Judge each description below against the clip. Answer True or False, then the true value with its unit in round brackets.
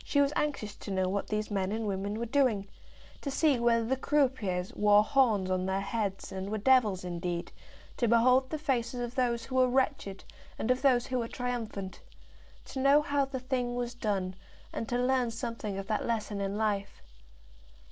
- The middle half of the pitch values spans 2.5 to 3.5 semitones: False (4.4 semitones)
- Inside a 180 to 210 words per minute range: True (190 wpm)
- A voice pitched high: True (230 Hz)